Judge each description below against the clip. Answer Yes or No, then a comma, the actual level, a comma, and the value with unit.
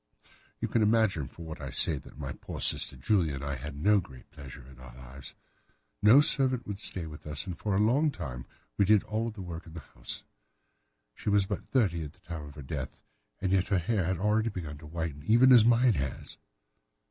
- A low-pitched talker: Yes, very low, 85 Hz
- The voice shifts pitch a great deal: Yes, wide, 6.7 semitones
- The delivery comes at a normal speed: No, fast, 220 wpm